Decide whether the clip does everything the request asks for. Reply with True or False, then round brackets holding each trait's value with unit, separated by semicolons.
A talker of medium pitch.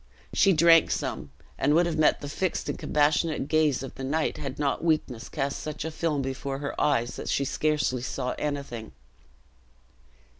True (145 Hz)